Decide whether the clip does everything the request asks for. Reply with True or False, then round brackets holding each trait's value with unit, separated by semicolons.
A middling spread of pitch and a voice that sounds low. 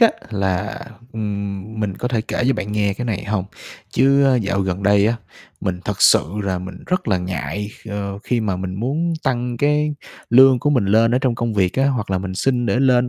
True (4.4 semitones; 110 Hz)